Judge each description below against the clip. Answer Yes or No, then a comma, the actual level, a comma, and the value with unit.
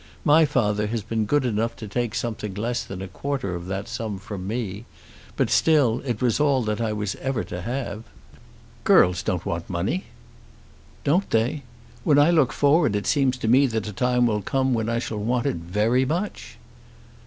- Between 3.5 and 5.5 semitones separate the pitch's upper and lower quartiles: Yes, average, 4.2 semitones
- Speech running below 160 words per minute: No, average, 190 wpm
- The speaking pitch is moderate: No, low, 115 Hz